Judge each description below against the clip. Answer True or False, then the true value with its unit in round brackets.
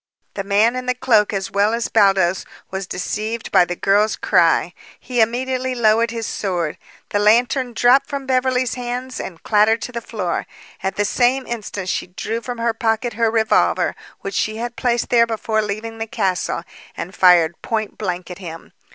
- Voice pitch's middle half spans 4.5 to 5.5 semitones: False (3.5 semitones)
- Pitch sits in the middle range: False (220 Hz)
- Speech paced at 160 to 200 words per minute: True (180 wpm)